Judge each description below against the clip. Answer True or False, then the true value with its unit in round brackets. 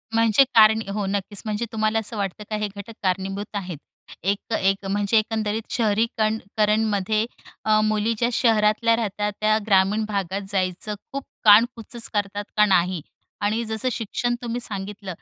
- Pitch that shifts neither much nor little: False (1.7 semitones)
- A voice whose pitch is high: True (210 Hz)